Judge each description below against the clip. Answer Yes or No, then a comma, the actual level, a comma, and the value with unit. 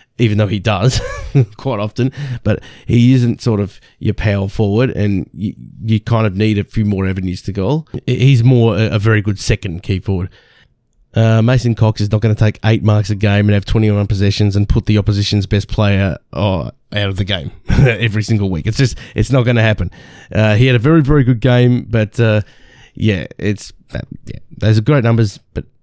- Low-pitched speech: Yes, low, 110 Hz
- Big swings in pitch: No, narrow, 2.6 semitones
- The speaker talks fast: Yes, fast, 210 wpm